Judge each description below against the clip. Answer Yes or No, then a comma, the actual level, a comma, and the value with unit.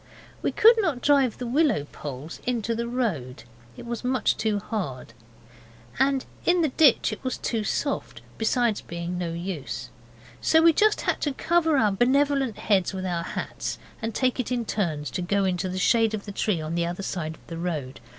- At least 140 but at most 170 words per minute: No, average, 195 wpm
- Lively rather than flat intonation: Yes, wide, 6.9 semitones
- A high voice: Yes, high, 215 Hz